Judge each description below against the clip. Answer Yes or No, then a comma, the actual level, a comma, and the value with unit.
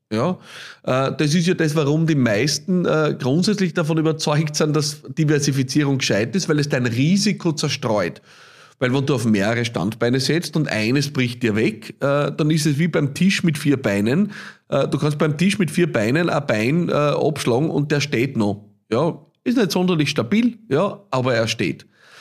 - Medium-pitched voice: Yes, medium, 150 Hz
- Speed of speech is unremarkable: Yes, average, 175 wpm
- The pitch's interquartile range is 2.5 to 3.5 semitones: No, average, 4.3 semitones